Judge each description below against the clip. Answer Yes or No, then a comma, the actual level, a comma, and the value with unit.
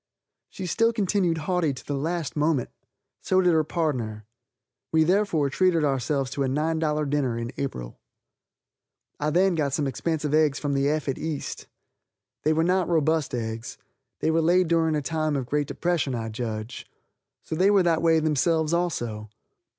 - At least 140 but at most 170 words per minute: Yes, average, 165 wpm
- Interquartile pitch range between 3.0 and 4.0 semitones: Yes, average, 3.5 semitones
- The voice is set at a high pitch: No, medium, 155 Hz